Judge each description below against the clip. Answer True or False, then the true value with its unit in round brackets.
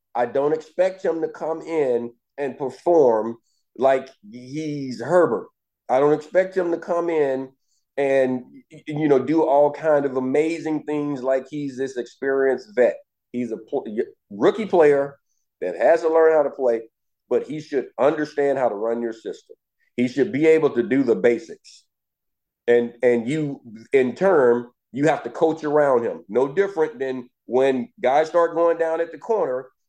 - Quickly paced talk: False (170 wpm)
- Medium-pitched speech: True (145 Hz)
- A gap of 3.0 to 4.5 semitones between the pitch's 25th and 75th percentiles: True (3.8 semitones)